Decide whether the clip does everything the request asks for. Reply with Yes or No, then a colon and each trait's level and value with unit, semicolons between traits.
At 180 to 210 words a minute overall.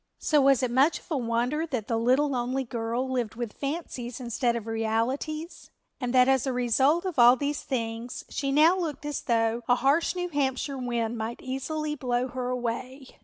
Yes: average, 190 wpm